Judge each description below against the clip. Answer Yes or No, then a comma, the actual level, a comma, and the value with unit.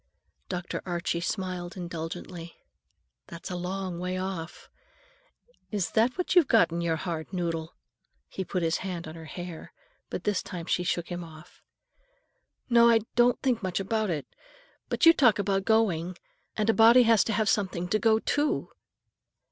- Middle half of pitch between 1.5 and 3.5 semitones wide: No, average, 4.4 semitones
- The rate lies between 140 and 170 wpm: Yes, average, 165 wpm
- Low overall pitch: No, medium, 185 Hz